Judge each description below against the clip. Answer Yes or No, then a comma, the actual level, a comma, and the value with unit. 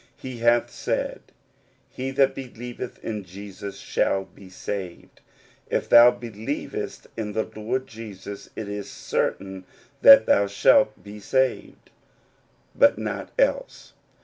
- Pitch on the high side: No, low, 110 Hz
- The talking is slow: Yes, slow, 130 wpm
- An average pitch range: Yes, average, 3.5 semitones